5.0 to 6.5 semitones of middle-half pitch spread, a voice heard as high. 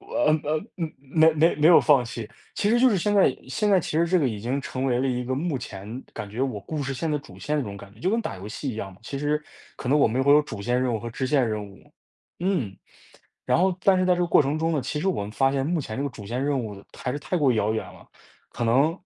No: wide, 5.4 semitones; low, 135 Hz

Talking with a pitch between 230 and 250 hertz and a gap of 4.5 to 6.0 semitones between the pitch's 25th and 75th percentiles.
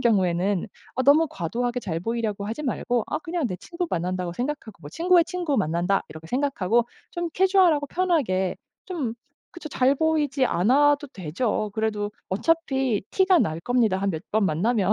No: high, 240 Hz; wide, 7.7 semitones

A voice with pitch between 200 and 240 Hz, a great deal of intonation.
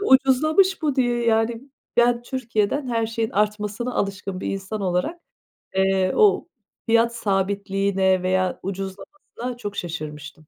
No: high, 210 Hz; average, 4.0 semitones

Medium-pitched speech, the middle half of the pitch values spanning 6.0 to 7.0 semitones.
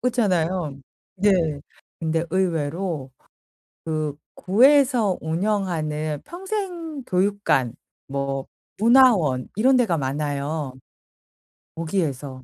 Yes: medium, 170 Hz; wide, 6.7 semitones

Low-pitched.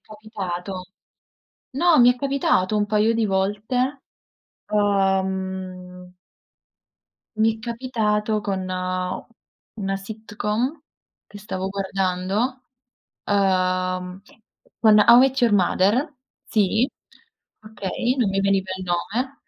No: high, 205 Hz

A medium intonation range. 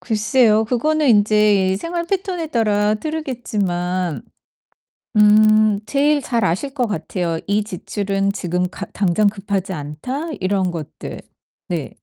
Yes: average, 4.9 semitones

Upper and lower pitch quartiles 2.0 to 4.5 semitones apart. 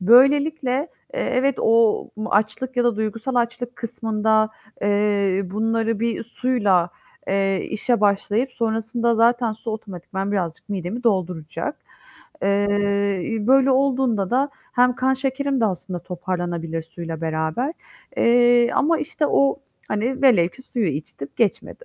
Yes: average, 4.2 semitones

